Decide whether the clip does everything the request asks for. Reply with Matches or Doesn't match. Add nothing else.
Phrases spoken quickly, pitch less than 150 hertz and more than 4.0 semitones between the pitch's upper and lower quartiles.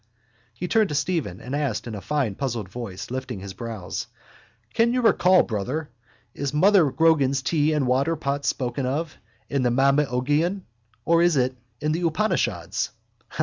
Doesn't match